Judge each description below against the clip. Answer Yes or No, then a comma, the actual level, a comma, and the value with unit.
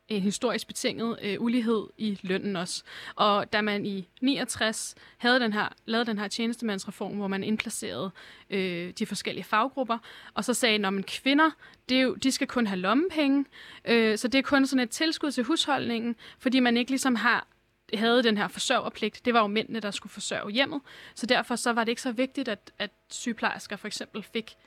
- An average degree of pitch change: Yes, average, 3.3 semitones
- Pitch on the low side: No, high, 230 Hz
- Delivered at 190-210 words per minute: Yes, average, 205 wpm